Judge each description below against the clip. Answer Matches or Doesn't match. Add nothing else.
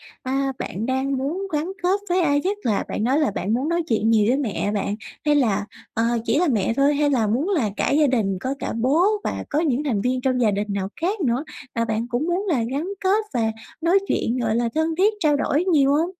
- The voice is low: Doesn't match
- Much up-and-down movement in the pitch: Matches